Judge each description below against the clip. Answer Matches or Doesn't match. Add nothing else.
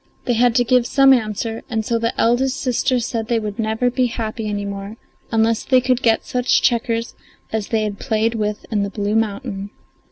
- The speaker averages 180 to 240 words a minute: Matches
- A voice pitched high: Matches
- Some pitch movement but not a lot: Doesn't match